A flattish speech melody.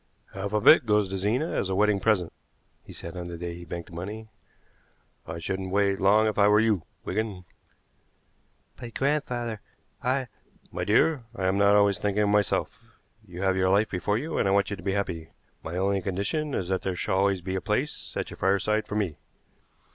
Yes: narrow, 2.3 semitones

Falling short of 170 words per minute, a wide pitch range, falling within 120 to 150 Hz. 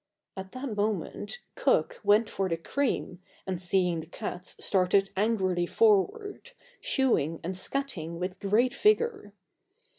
No: average, 140 wpm; wide, 7.0 semitones; high, 205 Hz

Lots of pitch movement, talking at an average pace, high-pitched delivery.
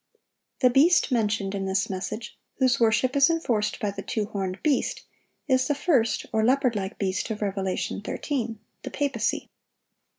No: average, 4.7 semitones; average, 155 wpm; high, 225 Hz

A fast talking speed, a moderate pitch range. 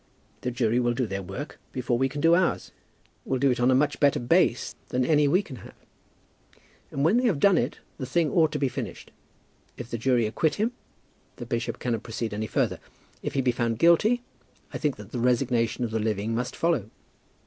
Yes: fast, 215 wpm; average, 4.2 semitones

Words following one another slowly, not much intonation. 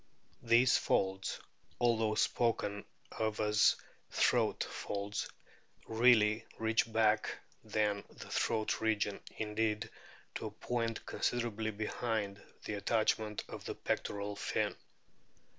Yes: slow, 110 wpm; narrow, 1.5 semitones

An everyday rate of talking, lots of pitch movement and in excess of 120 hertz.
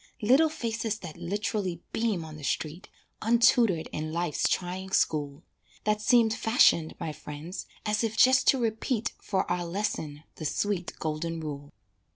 Yes: average, 150 wpm; wide, 5.8 semitones; medium, 185 Hz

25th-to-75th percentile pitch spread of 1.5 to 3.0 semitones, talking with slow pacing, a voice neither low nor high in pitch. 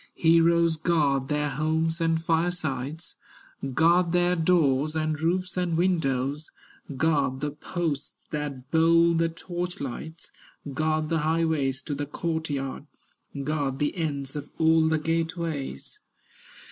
Yes: narrow, 2.5 semitones; slow, 130 wpm; medium, 160 Hz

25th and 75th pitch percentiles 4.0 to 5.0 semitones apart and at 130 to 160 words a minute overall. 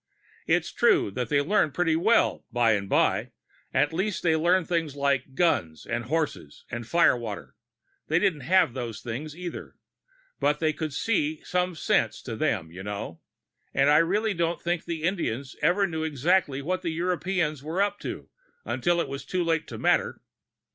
No: average, 4.7 semitones; average, 175 wpm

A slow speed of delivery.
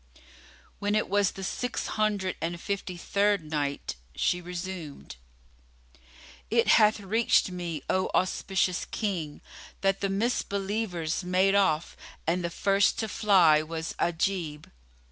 Yes: slow, 125 wpm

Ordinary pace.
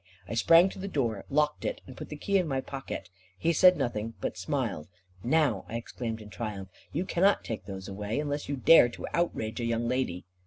No: fast, 210 wpm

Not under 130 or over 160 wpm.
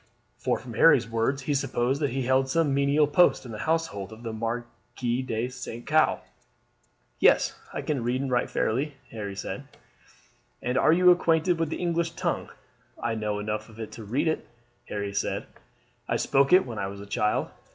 No: average, 195 wpm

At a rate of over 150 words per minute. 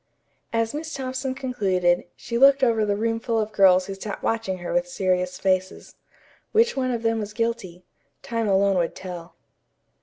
Yes: average, 170 wpm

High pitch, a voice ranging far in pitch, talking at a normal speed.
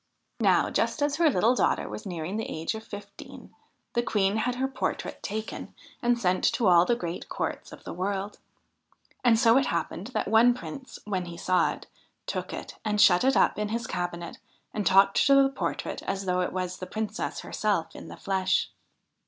No: high, 205 Hz; average, 4.4 semitones; average, 195 wpm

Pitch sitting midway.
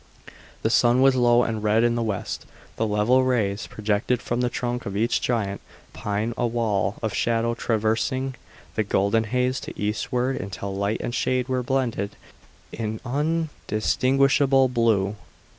No: low, 115 Hz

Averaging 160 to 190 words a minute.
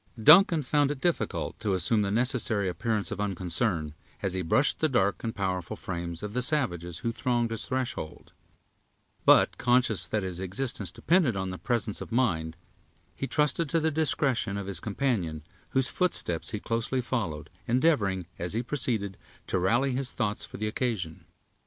Yes: average, 170 wpm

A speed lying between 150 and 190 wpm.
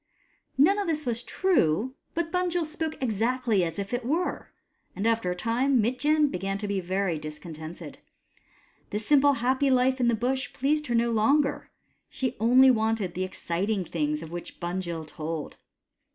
Yes: average, 165 wpm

